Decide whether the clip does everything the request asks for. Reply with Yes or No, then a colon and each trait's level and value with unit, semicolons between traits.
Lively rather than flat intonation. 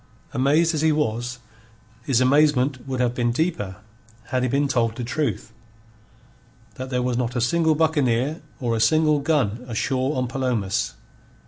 No: average, 3.7 semitones